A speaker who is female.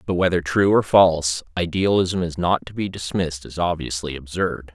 No: male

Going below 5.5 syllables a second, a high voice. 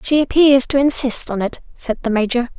Yes: 5.2 syllables/s; very high, 255 Hz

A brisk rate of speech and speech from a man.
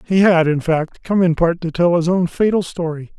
Yes: fast, 245 wpm; male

